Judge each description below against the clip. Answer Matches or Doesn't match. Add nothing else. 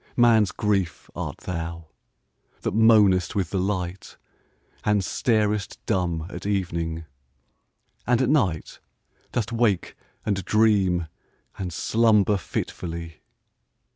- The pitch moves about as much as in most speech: Matches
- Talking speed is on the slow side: Matches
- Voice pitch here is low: Matches